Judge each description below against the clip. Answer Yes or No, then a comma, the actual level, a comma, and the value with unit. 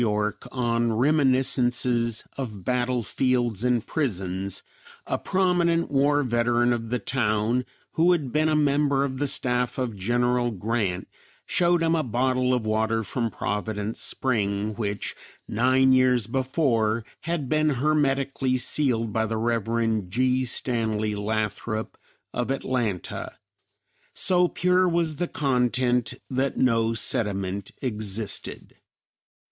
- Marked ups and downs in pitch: No, average, 3.6 semitones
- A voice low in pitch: Yes, low, 120 Hz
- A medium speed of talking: No, slow, 120 wpm